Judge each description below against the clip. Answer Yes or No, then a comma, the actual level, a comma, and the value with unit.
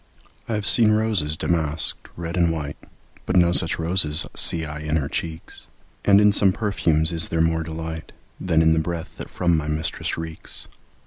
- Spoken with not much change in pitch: Yes, narrow, 2.1 semitones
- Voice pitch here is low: Yes, very low, 80 Hz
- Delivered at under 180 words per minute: No, average, 185 wpm